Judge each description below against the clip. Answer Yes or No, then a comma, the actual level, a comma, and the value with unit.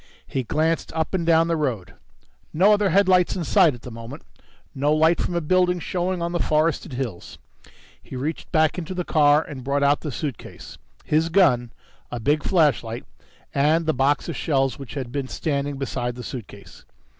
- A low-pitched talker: No, medium, 150 Hz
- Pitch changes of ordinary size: Yes, average, 4.0 semitones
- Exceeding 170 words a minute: Yes, average, 185 wpm